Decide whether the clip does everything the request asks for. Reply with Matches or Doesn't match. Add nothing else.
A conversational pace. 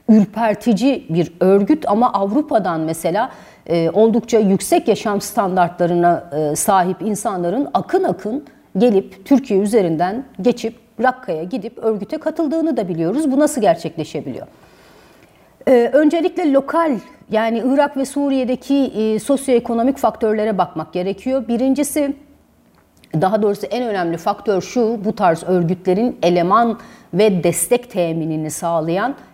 Matches